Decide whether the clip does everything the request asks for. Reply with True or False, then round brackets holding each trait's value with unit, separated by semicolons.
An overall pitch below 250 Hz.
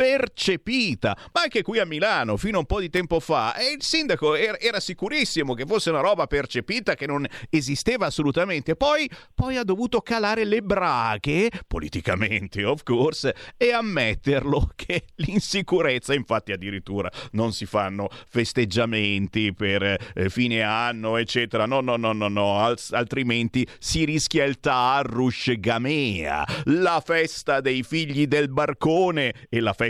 True (140 Hz)